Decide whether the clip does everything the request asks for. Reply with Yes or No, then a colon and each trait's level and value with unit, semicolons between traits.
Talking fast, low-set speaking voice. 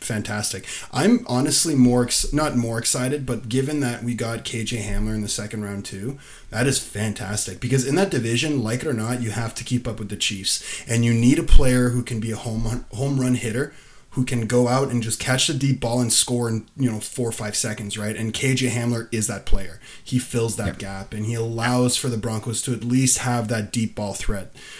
Yes: fast, 230 wpm; low, 120 Hz